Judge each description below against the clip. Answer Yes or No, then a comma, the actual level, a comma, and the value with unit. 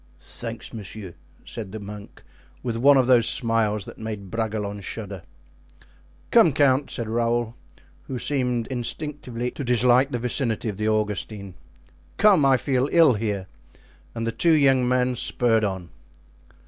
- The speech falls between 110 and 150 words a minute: Yes, average, 145 wpm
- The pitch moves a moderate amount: Yes, average, 3.3 semitones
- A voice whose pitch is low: Yes, low, 115 Hz